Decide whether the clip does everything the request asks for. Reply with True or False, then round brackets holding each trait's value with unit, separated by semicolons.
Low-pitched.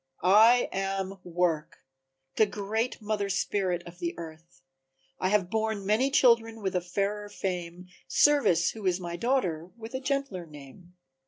False (195 Hz)